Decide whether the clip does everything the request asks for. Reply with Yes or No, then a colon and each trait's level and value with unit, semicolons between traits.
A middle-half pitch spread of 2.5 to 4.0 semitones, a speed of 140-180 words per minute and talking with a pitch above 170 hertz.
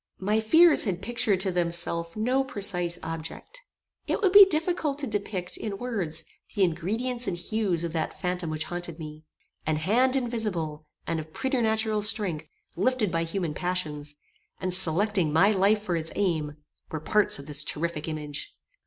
No: average, 5.2 semitones; average, 160 wpm; medium, 185 Hz